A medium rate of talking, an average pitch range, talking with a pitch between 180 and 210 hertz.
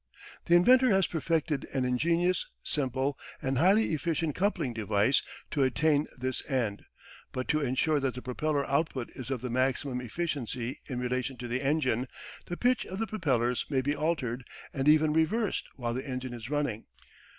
No: average, 170 wpm; average, 4.1 semitones; low, 135 Hz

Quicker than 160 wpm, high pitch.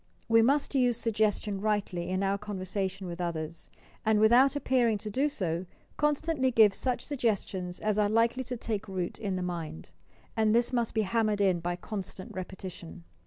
Yes: average, 175 wpm; high, 210 Hz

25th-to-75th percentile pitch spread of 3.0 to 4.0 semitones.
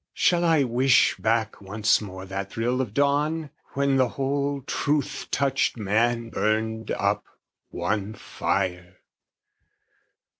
No: average, 4.7 semitones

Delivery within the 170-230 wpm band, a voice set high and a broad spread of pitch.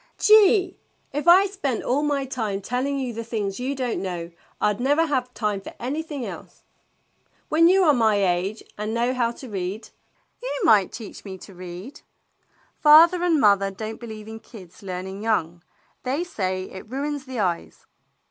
Yes: average, 185 wpm; high, 235 Hz; wide, 6.5 semitones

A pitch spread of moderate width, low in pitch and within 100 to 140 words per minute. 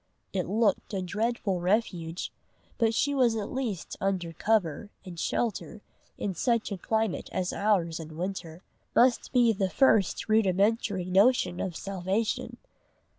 No: average, 3.8 semitones; high, 200 Hz; slow, 135 wpm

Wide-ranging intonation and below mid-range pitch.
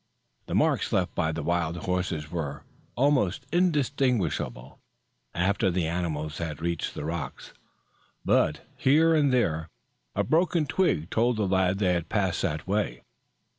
Yes: wide, 7.5 semitones; very low, 90 Hz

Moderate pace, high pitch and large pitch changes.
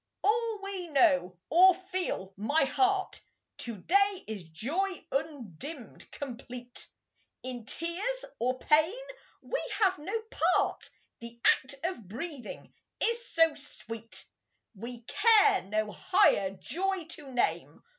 No: slow, 115 wpm; very high, 305 Hz; wide, 8.4 semitones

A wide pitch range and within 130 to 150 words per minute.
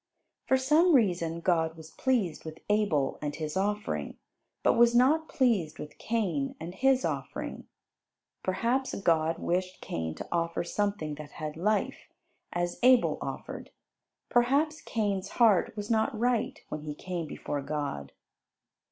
Yes: wide, 7.0 semitones; average, 140 wpm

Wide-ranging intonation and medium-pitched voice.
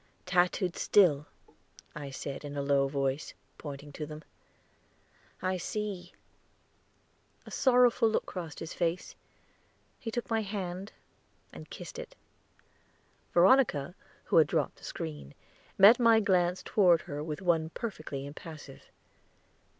Yes: wide, 5.7 semitones; medium, 175 Hz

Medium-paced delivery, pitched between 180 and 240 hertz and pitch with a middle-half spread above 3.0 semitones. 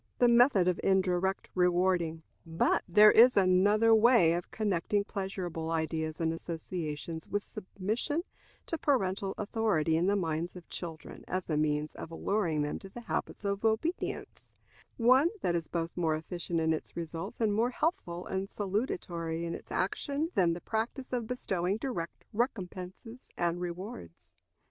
Yes: average, 155 wpm; medium, 185 Hz; average, 4.5 semitones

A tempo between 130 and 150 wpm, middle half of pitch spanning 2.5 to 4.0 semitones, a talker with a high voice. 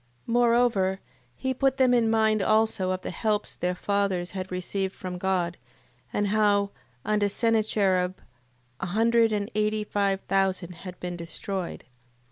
Yes: average, 145 wpm; average, 2.9 semitones; high, 200 Hz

